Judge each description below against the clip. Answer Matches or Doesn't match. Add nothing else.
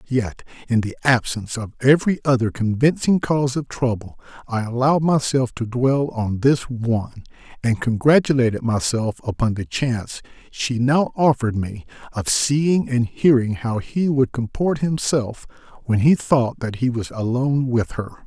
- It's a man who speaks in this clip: Matches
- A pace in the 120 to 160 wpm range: Matches